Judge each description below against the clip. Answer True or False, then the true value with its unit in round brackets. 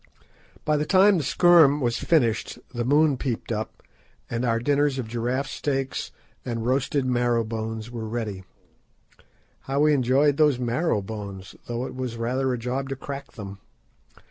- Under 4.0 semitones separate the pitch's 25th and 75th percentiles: True (3.5 semitones)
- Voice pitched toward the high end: False (125 Hz)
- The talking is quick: False (160 wpm)